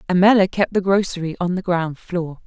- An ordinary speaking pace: Yes, average, 195 wpm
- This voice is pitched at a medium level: Yes, medium, 180 Hz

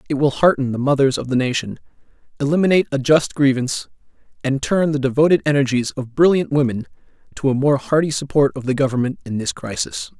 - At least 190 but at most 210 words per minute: No, average, 180 wpm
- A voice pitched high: No, medium, 140 Hz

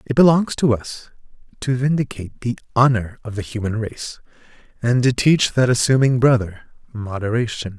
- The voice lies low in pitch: Yes, low, 120 Hz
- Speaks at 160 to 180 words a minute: No, average, 145 wpm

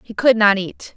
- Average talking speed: No, fast, 250 wpm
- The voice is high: Yes, high, 215 Hz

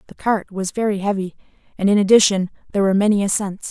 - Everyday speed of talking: Yes, average, 195 wpm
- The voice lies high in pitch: Yes, high, 200 Hz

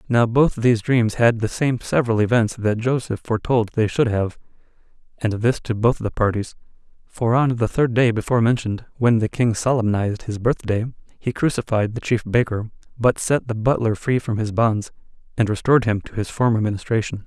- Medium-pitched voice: No, low, 115 Hz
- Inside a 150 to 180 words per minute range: No, average, 190 wpm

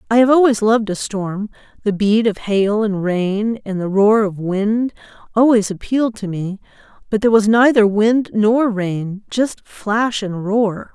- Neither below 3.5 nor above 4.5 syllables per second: Yes, 4.1 syllables/s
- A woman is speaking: Yes, female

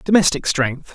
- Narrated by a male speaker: Yes, male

